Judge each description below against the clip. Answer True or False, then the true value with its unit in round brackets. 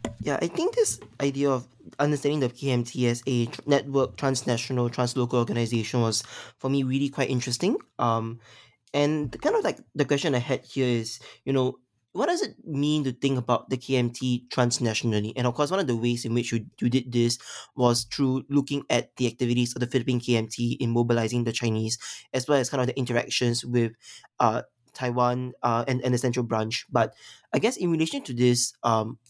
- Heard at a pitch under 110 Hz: False (125 Hz)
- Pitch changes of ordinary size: False (2.3 semitones)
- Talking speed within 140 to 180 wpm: False (195 wpm)